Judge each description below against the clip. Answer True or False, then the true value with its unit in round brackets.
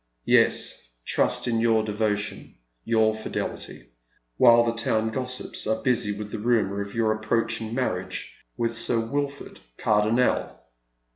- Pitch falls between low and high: False (110 Hz)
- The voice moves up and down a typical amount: False (1.7 semitones)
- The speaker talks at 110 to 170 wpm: True (140 wpm)